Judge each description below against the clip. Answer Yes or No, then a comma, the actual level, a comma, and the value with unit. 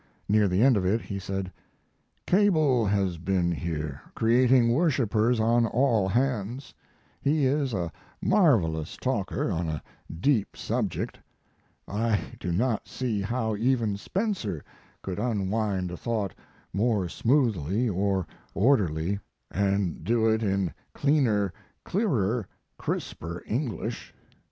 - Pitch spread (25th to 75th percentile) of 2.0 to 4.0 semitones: No, average, 4.8 semitones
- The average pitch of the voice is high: No, low, 110 Hz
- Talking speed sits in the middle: No, slow, 115 wpm